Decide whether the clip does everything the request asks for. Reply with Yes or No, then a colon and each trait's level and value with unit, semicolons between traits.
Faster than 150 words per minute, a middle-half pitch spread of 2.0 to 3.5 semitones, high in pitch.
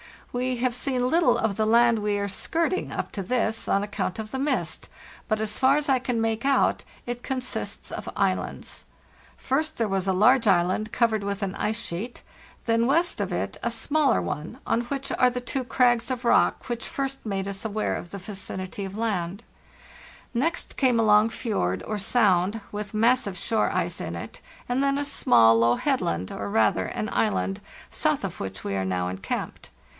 No: average, 190 wpm; average, 4.6 semitones; high, 220 Hz